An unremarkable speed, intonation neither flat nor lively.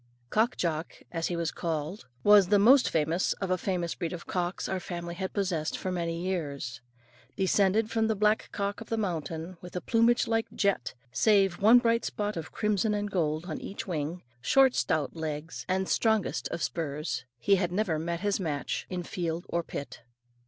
Yes: average, 185 wpm; average, 4.0 semitones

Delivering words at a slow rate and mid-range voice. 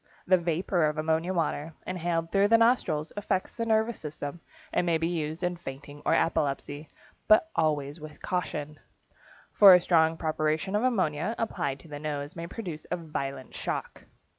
No: average, 165 wpm; medium, 165 Hz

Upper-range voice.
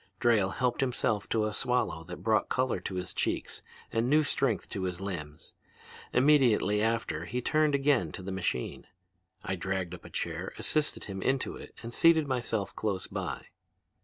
No: low, 110 Hz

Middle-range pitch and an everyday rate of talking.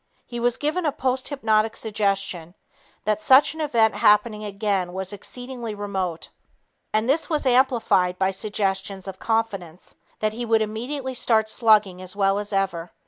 No: high, 215 Hz; average, 150 wpm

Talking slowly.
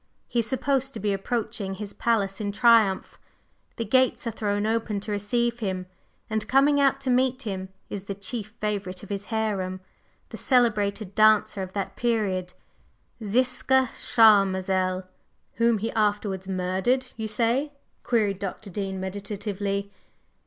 No: average, 145 wpm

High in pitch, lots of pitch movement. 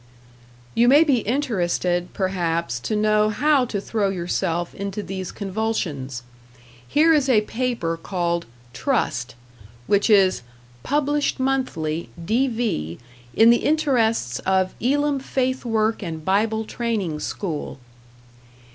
Yes: high, 210 Hz; wide, 6.3 semitones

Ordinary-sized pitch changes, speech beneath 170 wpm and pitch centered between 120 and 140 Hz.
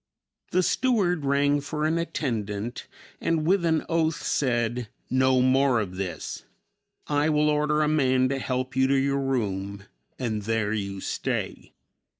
Yes: average, 4.8 semitones; average, 150 wpm; low, 135 Hz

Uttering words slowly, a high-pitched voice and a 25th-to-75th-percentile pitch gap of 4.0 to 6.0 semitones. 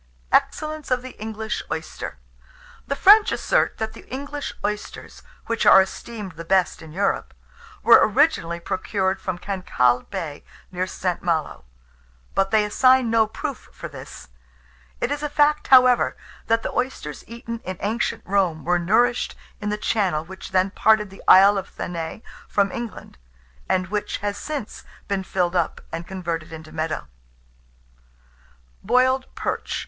No: average, 150 wpm; high, 205 Hz; average, 4.9 semitones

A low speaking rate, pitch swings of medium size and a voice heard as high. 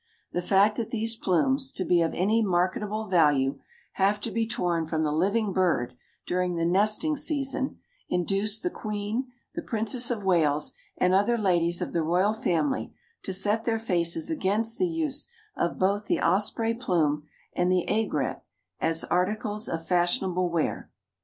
No: average, 160 wpm; average, 4.3 semitones; high, 195 Hz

